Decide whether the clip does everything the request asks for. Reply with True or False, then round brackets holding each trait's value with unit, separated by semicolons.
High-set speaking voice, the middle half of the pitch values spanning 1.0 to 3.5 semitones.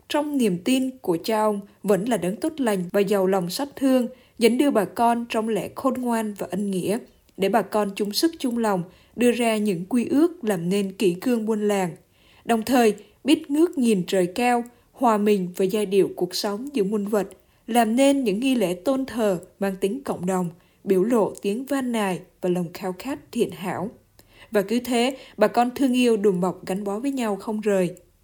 False (215 Hz; 4.1 semitones)